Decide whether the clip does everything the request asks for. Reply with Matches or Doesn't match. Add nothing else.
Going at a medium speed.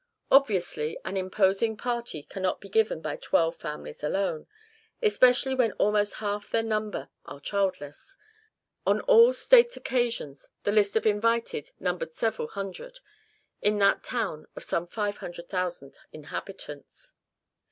Doesn't match